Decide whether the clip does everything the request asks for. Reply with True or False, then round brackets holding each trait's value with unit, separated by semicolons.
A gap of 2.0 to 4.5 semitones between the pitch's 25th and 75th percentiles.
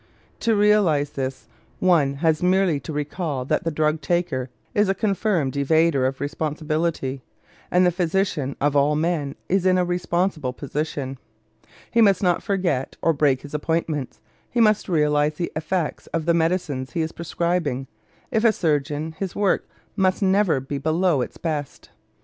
True (4.0 semitones)